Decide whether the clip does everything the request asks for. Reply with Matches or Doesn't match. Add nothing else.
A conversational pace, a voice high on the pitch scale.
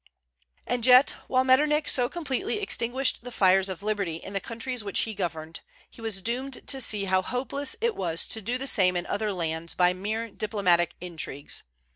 Matches